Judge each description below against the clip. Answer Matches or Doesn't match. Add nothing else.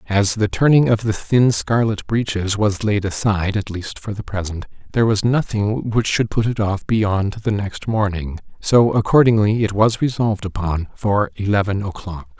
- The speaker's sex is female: Doesn't match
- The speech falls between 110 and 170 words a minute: Doesn't match